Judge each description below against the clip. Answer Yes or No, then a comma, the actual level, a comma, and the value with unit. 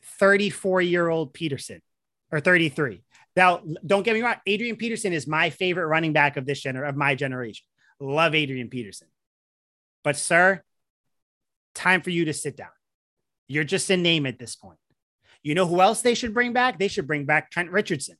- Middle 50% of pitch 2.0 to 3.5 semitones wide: No, average, 4.8 semitones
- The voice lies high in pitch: No, medium, 165 Hz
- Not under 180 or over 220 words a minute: Yes, average, 185 wpm